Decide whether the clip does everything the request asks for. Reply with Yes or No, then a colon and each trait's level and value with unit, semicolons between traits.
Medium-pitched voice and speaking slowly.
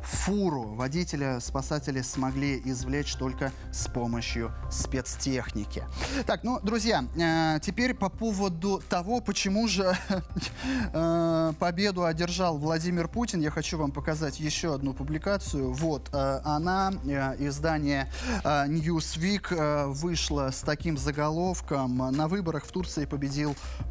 Yes: medium, 155 Hz; slow, 105 wpm